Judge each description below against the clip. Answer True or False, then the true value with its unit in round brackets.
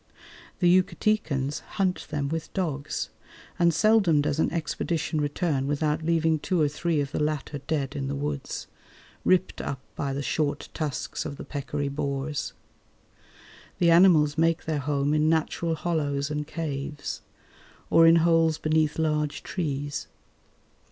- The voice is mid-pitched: True (155 Hz)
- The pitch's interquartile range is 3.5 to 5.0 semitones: False (2.4 semitones)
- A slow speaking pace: False (145 wpm)